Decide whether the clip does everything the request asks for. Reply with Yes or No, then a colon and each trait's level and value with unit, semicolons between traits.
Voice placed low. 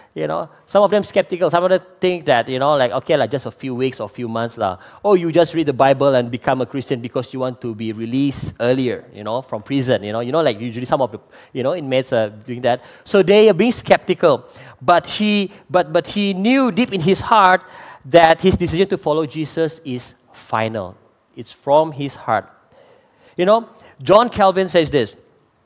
No: medium, 150 Hz